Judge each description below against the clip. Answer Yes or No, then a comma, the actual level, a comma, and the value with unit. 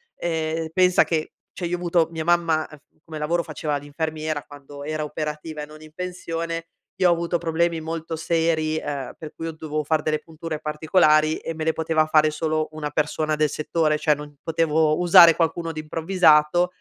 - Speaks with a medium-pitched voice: Yes, medium, 160 Hz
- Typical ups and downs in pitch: No, narrow, 1.4 semitones